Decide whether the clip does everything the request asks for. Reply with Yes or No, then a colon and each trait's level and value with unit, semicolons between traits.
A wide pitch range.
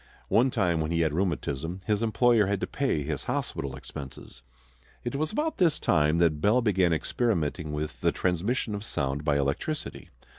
Yes: wide, 7.2 semitones